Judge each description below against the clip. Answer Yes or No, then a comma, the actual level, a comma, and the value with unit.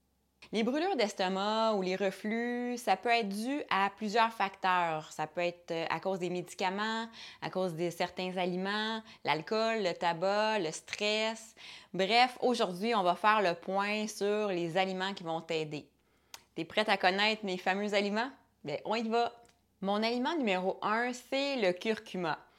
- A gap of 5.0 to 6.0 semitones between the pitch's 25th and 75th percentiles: No, average, 3.5 semitones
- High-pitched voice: Yes, high, 200 Hz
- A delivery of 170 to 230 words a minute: No, average, 160 wpm